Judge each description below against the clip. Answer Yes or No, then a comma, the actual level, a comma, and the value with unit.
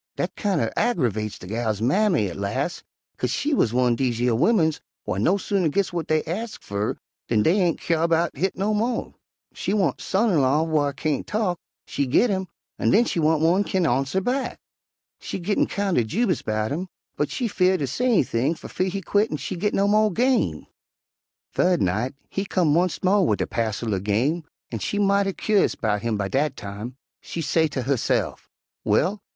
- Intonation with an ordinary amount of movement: No, wide, 8.2 semitones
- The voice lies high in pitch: No, medium, 165 Hz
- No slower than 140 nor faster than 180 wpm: No, fast, 205 wpm